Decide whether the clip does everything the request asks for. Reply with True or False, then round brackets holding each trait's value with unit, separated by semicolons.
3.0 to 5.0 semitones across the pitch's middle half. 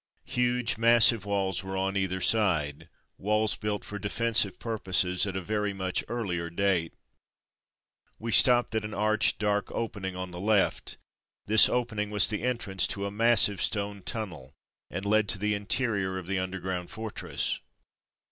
False (2.5 semitones)